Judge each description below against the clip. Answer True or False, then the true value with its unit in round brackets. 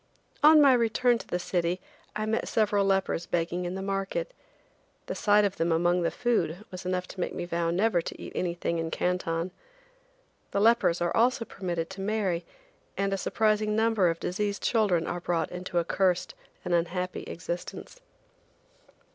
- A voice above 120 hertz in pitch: True (185 Hz)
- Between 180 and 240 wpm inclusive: False (170 wpm)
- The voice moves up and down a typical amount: True (3.5 semitones)